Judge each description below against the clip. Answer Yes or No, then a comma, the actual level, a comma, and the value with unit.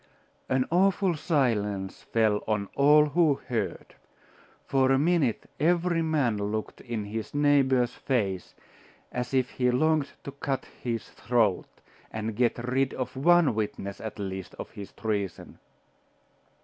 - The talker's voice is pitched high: No, low, 125 Hz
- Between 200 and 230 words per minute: No, slow, 135 wpm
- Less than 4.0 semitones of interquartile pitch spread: No, average, 5.1 semitones